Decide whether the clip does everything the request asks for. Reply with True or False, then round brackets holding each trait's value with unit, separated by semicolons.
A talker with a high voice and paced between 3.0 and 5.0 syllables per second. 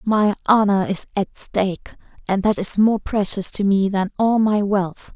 True (200 Hz; 4.2 syllables/s)